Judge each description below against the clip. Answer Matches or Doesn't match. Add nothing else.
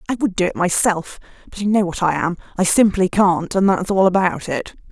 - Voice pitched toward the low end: Doesn't match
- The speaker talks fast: Matches